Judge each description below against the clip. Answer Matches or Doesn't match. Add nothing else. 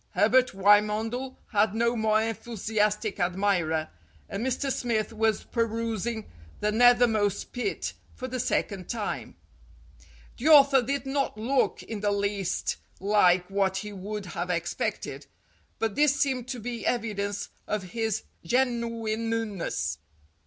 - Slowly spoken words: Matches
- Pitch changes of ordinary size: Matches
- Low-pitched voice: Doesn't match